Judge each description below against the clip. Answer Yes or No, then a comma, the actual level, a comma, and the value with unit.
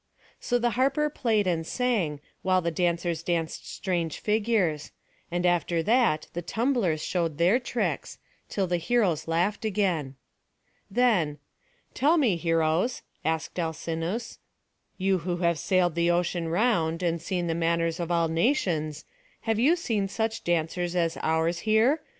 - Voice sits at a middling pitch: Yes, medium, 175 Hz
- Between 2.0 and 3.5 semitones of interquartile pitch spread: No, average, 4.9 semitones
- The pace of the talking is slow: No, average, 145 wpm